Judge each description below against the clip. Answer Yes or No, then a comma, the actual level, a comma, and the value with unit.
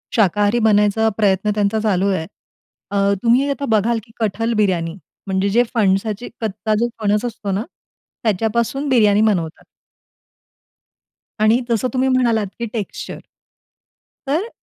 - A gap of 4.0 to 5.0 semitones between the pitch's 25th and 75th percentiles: No, average, 2.7 semitones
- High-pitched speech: Yes, high, 215 Hz